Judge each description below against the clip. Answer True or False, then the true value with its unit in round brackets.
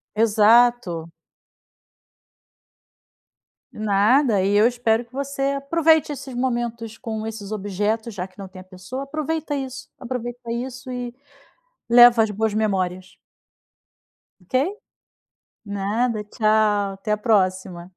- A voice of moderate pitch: False (225 Hz)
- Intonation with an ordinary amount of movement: True (3.7 semitones)